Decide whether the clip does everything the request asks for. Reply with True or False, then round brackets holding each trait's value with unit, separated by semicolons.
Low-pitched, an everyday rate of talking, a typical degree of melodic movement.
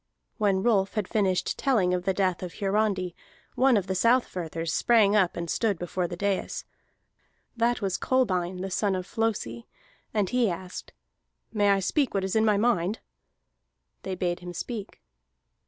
False (195 Hz; 165 wpm; 3.3 semitones)